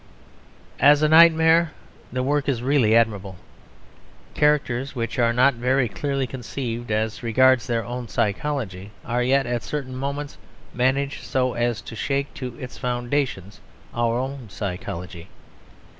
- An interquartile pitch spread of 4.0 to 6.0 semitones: No, average, 3.1 semitones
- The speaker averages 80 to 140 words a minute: Yes, slow, 135 wpm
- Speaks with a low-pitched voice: Yes, low, 125 Hz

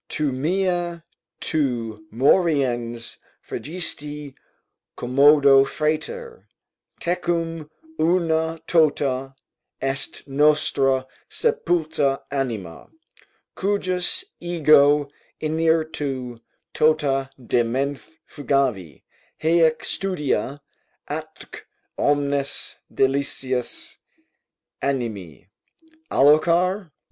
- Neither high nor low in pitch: Yes, medium, 145 Hz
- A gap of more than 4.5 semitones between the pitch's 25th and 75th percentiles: No, average, 3.5 semitones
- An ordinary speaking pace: No, slow, 60 wpm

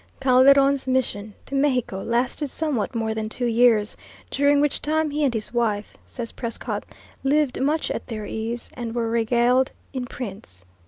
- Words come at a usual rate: Yes, average, 160 wpm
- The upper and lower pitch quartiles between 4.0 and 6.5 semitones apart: No, average, 3.5 semitones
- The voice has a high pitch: Yes, high, 245 Hz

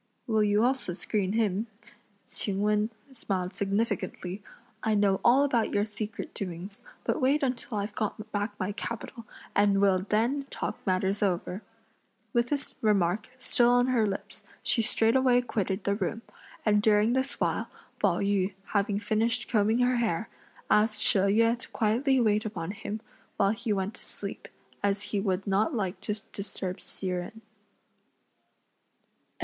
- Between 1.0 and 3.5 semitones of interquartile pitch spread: Yes, narrow, 2.6 semitones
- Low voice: No, high, 210 Hz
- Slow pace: No, average, 155 wpm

